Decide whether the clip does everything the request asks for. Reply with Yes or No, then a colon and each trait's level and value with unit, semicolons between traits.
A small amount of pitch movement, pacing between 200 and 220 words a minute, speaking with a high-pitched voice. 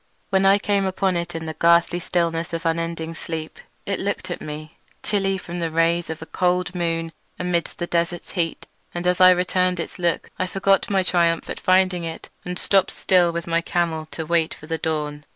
No: narrow, 1.7 semitones; fast, 205 wpm; medium, 170 Hz